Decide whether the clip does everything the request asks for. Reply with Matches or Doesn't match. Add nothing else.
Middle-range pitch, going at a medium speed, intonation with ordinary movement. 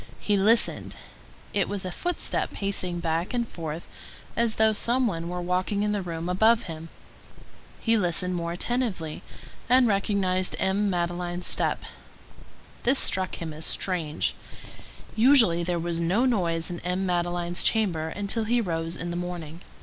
Matches